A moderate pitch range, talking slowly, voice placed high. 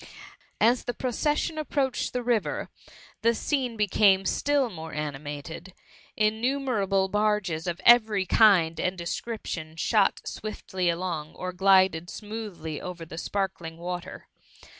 Yes: average, 4.9 semitones; slow, 120 wpm; high, 195 Hz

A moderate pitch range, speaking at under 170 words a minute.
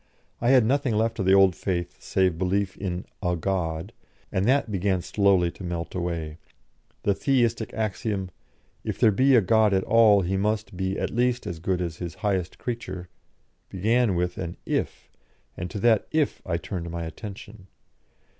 No: average, 3.8 semitones; average, 175 wpm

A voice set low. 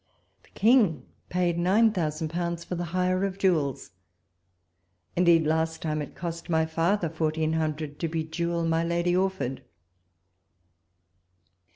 No: medium, 170 Hz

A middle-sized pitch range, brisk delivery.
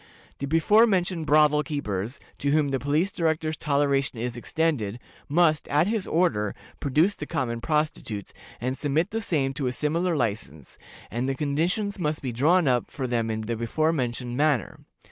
No: average, 4.8 semitones; average, 170 wpm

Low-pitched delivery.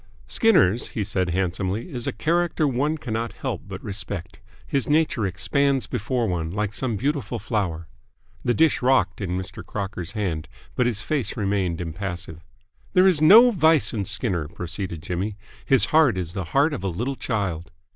Yes: low, 105 Hz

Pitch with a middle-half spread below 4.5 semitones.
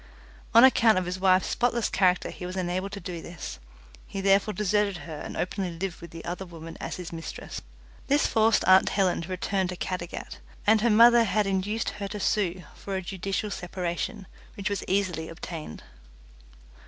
Yes: average, 2.8 semitones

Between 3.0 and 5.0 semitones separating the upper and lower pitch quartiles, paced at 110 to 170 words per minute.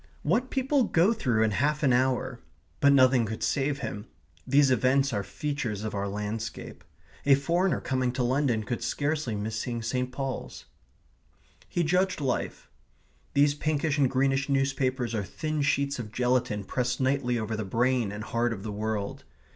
Yes: average, 4.2 semitones; average, 165 wpm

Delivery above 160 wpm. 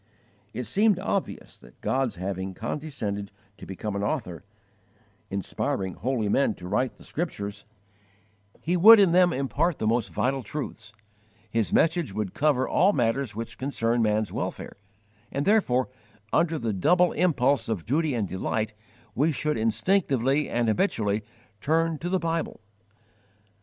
No: average, 140 wpm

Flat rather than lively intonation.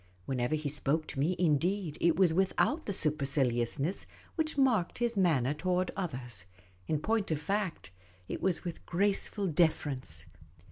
No: wide, 5.4 semitones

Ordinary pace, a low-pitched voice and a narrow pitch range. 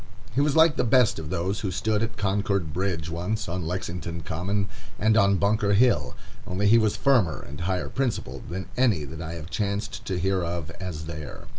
No: average, 195 wpm; very low, 95 Hz; average, 4.2 semitones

